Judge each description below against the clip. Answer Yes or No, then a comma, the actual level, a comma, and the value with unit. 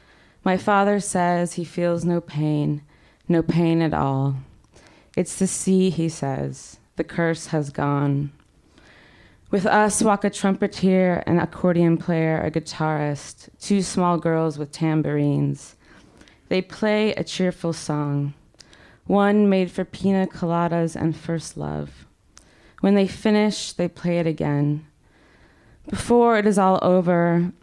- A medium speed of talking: No, slow, 130 wpm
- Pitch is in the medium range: Yes, medium, 170 Hz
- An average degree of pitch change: Yes, average, 4.0 semitones